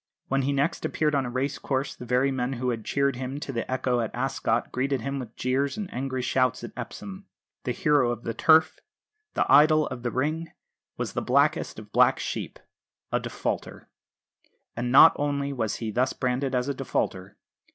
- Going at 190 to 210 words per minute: Yes, average, 195 wpm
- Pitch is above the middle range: No, low, 130 Hz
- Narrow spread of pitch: Yes, narrow, 2.3 semitones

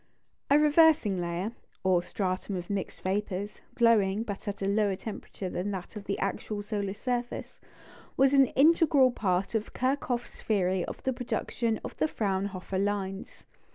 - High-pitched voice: Yes, high, 205 Hz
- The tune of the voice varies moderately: Yes, average, 4.0 semitones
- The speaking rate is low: No, average, 155 wpm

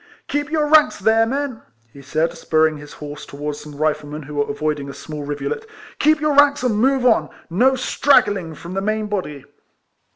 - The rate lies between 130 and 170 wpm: No, average, 195 wpm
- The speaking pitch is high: No, medium, 175 Hz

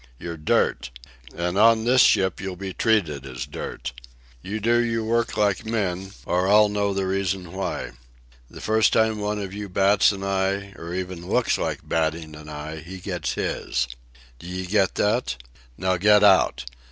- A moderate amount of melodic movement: Yes, average, 3.0 semitones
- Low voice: Yes, very low, 95 Hz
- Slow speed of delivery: No, average, 170 wpm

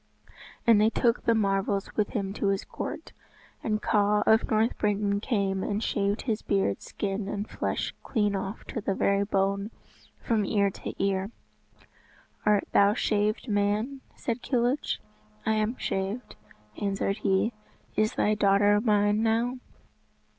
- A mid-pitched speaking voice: No, high, 205 Hz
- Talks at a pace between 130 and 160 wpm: Yes, average, 145 wpm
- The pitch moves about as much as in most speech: No, narrow, 1.8 semitones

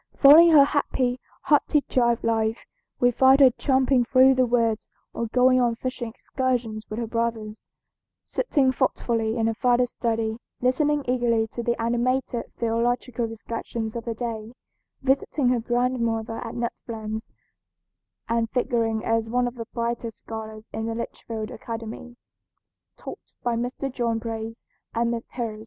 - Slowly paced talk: No, average, 145 wpm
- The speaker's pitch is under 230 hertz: No, high, 235 Hz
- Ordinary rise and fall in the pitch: No, narrow, 1.9 semitones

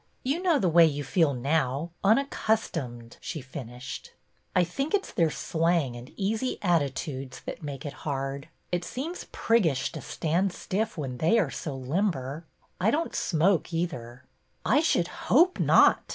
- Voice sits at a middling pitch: Yes, medium, 165 Hz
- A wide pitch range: Yes, wide, 6.9 semitones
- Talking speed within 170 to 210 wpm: No, average, 160 wpm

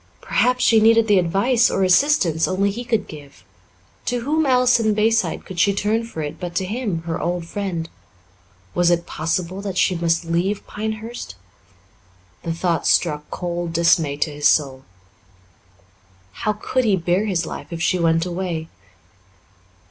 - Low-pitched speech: No, medium, 180 Hz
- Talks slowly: No, average, 160 wpm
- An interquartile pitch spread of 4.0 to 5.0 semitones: Yes, average, 4.7 semitones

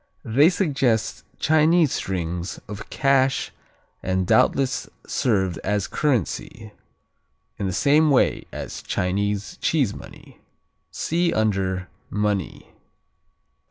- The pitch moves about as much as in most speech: No, wide, 6.5 semitones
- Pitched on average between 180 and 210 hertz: No, low, 110 Hz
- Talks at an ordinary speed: No, slow, 95 wpm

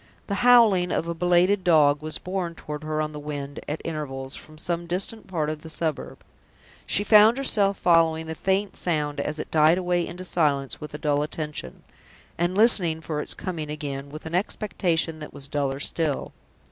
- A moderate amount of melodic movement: Yes, average, 3.2 semitones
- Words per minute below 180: No, average, 185 wpm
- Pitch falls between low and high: Yes, medium, 160 Hz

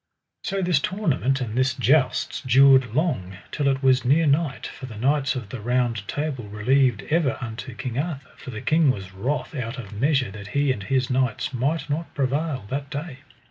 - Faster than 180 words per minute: Yes, average, 190 wpm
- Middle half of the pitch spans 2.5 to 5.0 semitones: Yes, average, 3.0 semitones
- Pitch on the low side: Yes, low, 130 Hz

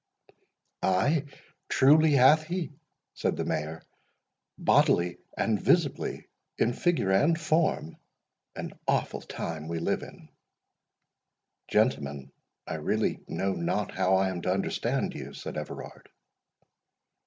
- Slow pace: Yes, slow, 110 wpm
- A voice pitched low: Yes, very low, 95 Hz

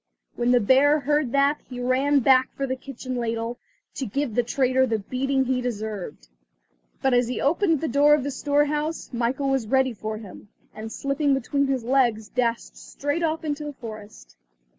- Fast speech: No, average, 185 wpm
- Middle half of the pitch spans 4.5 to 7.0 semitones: No, average, 3.3 semitones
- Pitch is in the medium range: No, very high, 260 Hz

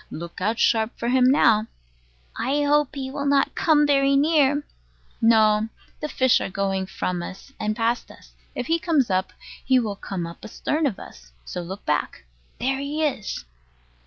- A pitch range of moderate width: No, wide, 6.1 semitones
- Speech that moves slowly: No, average, 175 wpm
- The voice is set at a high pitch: Yes, high, 240 Hz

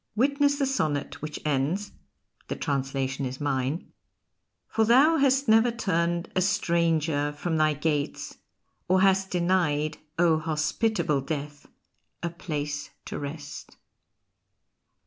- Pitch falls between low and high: Yes, medium, 160 Hz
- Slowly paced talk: Yes, slow, 115 wpm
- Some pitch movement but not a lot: Yes, average, 4.7 semitones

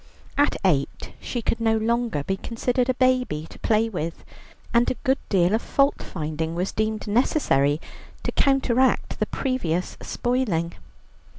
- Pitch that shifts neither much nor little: No, wide, 6.8 semitones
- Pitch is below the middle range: No, high, 225 Hz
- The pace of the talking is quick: No, average, 150 wpm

